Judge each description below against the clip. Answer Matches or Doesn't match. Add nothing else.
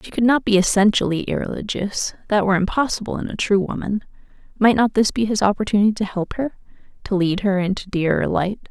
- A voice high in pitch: Matches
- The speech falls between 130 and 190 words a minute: Matches